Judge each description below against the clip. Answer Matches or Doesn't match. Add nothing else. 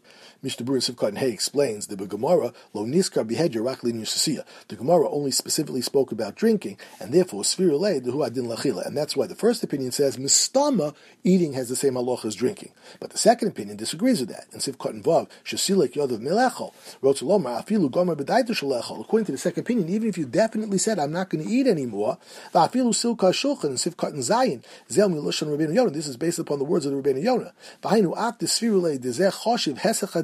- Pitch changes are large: Matches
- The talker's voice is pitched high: Doesn't match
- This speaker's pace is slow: Doesn't match